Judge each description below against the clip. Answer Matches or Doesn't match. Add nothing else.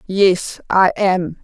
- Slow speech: Matches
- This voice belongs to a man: Doesn't match